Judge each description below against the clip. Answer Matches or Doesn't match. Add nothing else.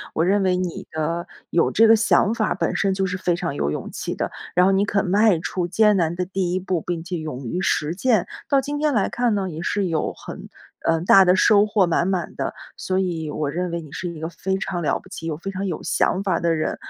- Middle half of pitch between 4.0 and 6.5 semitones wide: Doesn't match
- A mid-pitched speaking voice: Matches